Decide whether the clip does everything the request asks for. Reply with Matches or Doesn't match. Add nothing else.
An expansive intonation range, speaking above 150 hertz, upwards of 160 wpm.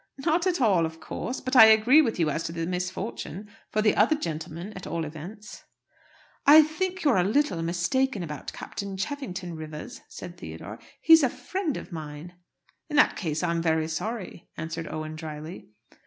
Matches